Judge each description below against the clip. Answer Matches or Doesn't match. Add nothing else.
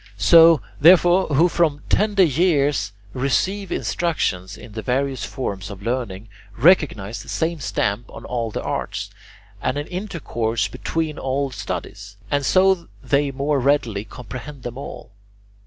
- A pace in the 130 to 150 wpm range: Matches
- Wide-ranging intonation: Matches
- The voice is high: Doesn't match